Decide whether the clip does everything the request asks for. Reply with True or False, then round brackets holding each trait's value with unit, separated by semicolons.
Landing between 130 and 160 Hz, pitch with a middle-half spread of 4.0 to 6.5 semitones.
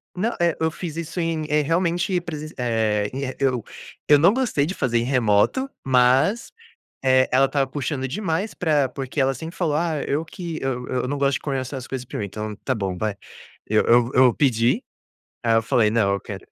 True (135 Hz; 4.8 semitones)